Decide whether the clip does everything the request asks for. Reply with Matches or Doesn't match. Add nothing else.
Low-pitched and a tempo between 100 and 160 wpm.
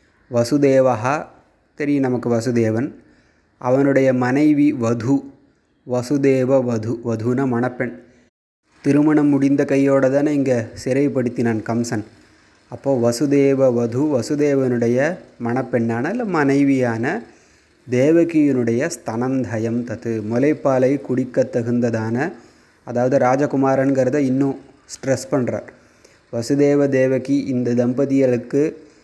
Doesn't match